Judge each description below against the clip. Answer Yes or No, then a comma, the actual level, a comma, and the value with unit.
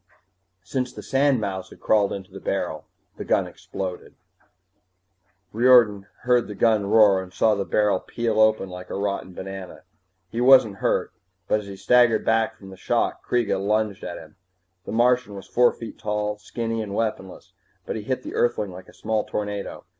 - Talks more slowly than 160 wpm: No, average, 175 wpm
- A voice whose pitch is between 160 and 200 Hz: No, low, 105 Hz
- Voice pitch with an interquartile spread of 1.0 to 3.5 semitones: Yes, average, 2.9 semitones